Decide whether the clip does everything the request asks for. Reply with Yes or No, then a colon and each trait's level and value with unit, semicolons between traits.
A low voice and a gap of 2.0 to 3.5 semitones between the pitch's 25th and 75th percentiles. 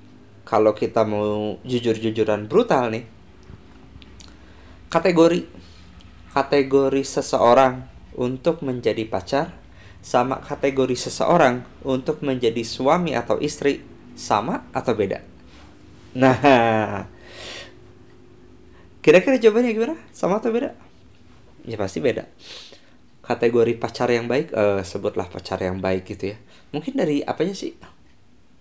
No: low, 120 Hz; average, 4.8 semitones